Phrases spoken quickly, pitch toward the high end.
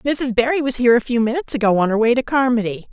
Yes: fast, 265 wpm; high, 240 Hz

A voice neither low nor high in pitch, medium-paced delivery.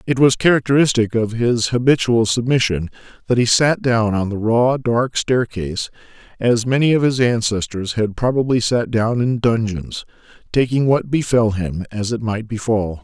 No: low, 115 Hz; average, 160 wpm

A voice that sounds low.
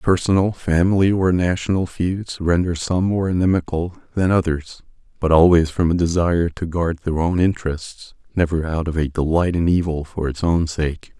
Yes: very low, 85 Hz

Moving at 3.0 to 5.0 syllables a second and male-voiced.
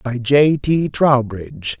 Yes: 3.6 syllables/s; male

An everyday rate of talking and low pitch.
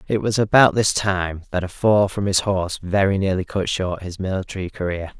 No: fast, 210 wpm; very low, 95 Hz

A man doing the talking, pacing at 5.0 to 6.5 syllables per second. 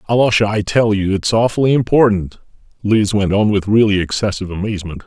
Yes: male; 6.1 syllables/s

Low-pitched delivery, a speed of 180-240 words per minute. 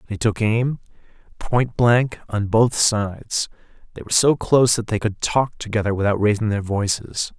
No: low, 110 Hz; average, 170 wpm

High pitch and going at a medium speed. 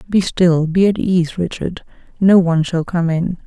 No: medium, 175 Hz; average, 190 wpm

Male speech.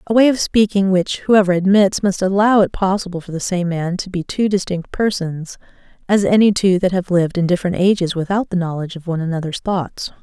No: female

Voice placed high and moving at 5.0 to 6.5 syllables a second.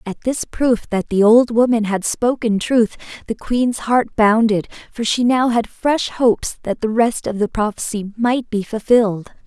No: high, 225 Hz; 4.4 syllables/s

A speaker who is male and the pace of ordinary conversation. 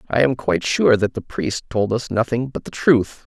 No: male; fast, 235 wpm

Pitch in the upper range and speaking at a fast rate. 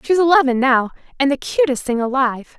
No: very high, 270 Hz; average, 185 wpm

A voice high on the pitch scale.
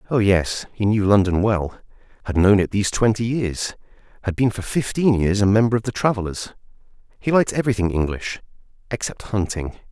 No: low, 105 Hz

